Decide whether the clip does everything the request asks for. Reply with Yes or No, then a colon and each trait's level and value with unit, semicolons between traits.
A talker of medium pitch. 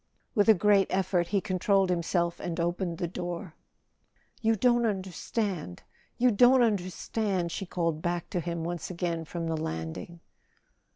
Yes: medium, 180 Hz